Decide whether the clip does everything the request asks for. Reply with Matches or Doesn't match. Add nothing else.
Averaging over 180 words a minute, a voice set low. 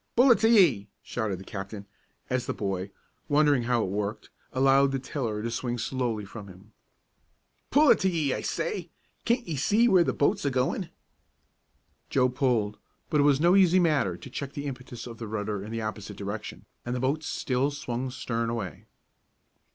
Matches